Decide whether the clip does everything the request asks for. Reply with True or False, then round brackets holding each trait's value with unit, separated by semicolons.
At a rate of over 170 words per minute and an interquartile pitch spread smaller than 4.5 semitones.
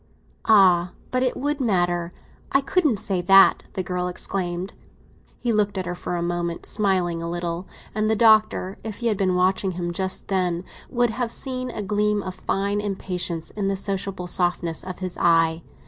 True (185 wpm; 3.1 semitones)